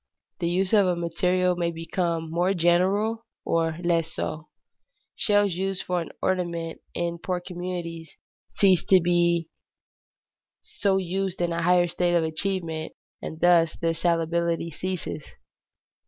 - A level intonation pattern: Yes, narrow, 1.8 semitones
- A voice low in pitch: No, medium, 175 Hz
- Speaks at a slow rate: Yes, slow, 130 wpm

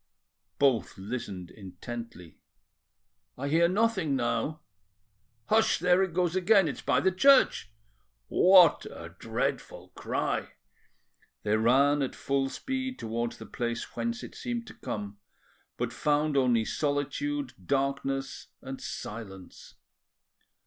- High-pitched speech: No, medium, 140 Hz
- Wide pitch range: Yes, wide, 7.8 semitones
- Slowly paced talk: Yes, slow, 115 wpm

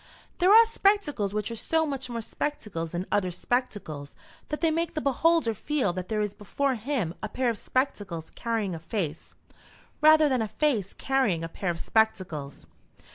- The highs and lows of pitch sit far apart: Yes, wide, 7.9 semitones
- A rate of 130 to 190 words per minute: Yes, average, 180 wpm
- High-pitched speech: Yes, high, 225 Hz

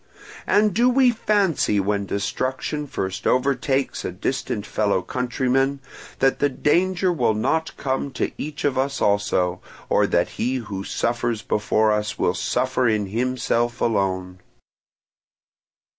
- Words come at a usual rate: No, slow, 130 wpm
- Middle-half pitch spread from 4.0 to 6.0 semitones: Yes, average, 5.3 semitones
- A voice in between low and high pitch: No, low, 125 Hz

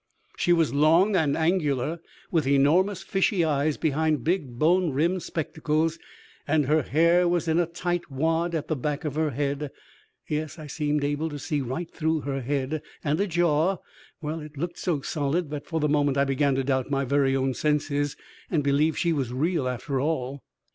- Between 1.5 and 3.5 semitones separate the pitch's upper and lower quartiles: Yes, average, 2.7 semitones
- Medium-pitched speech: Yes, medium, 150 Hz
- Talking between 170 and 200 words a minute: Yes, average, 185 wpm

